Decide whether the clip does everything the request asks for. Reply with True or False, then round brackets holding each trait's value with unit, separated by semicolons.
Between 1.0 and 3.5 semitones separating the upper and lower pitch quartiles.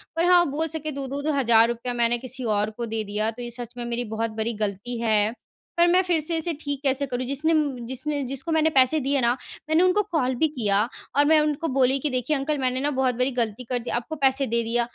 False (4.1 semitones)